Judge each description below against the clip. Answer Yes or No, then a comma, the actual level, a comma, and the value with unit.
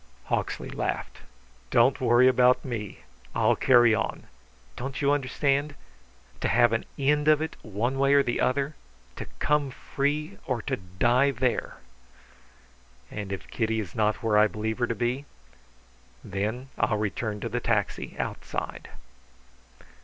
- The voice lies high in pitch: No, low, 120 Hz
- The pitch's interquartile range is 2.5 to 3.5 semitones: No, average, 4.1 semitones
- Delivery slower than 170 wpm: Yes, average, 145 wpm